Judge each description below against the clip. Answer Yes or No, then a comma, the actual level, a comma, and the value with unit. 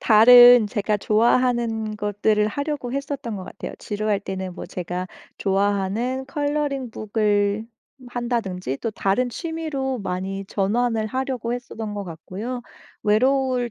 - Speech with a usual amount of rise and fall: Yes, average, 3.8 semitones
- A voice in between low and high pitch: No, high, 220 Hz